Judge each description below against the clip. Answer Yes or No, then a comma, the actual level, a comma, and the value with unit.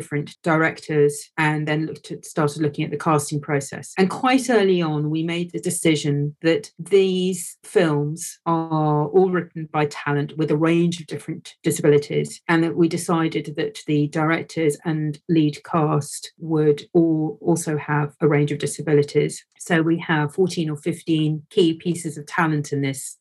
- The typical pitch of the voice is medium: Yes, medium, 155 Hz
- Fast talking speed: No, average, 165 wpm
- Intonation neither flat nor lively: No, narrow, 2.1 semitones